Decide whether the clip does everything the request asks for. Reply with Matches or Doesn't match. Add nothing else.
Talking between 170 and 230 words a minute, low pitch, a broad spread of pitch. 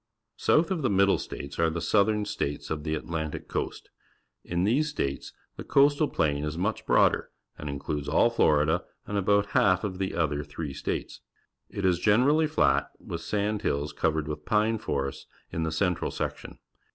Matches